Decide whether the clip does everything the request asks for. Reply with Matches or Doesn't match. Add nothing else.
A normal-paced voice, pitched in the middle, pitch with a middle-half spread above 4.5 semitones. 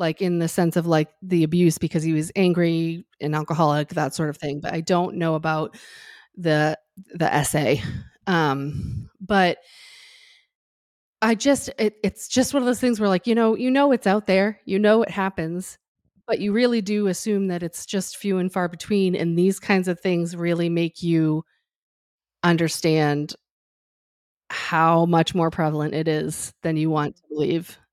Doesn't match